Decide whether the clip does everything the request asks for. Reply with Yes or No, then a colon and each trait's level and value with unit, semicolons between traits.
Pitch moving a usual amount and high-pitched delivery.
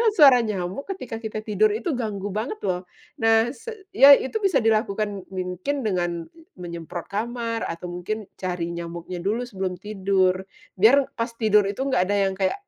Yes: average, 4.4 semitones; high, 210 Hz